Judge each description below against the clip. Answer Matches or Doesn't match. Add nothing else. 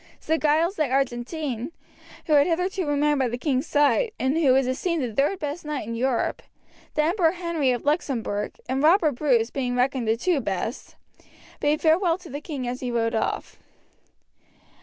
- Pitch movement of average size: Matches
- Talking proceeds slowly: Doesn't match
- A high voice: Matches